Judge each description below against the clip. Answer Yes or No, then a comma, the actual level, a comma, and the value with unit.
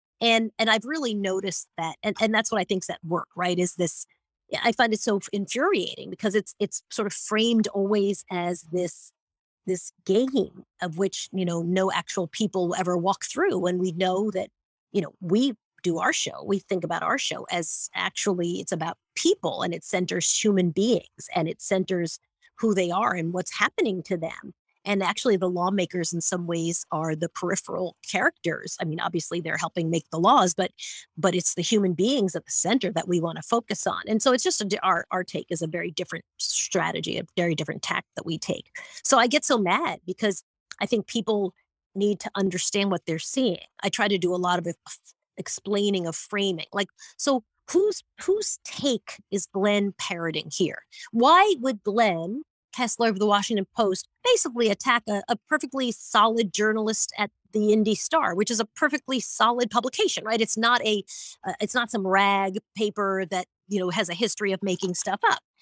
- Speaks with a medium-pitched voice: No, high, 200 Hz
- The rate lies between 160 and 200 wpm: Yes, average, 195 wpm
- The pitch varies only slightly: No, average, 3.8 semitones